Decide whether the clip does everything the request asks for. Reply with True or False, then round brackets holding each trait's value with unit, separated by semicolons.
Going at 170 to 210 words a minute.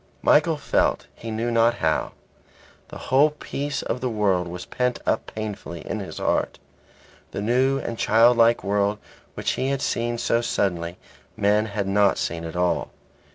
False (160 wpm)